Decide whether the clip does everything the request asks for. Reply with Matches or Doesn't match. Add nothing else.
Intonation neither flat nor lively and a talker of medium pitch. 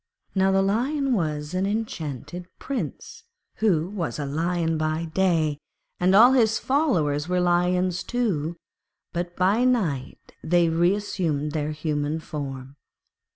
Matches